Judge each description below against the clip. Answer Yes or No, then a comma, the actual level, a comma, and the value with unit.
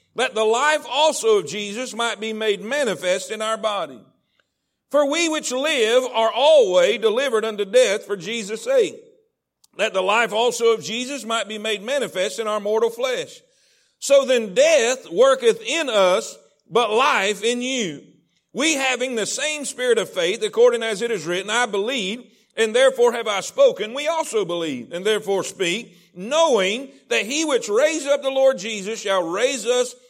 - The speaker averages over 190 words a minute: No, average, 170 wpm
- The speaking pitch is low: No, very high, 255 Hz